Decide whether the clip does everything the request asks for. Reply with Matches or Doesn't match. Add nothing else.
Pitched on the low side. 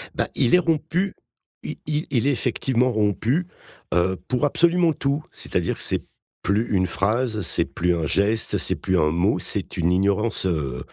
Matches